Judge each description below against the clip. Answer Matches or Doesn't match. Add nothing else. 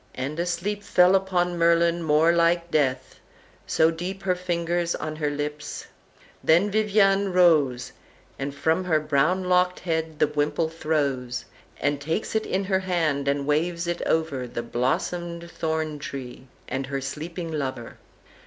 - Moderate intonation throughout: Matches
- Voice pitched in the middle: Matches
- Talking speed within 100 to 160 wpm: Matches